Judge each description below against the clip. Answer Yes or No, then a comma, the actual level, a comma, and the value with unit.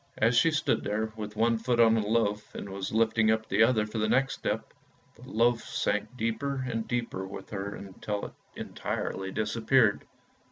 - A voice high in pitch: No, low, 110 Hz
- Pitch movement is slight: Yes, narrow, 1.7 semitones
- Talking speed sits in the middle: Yes, average, 185 wpm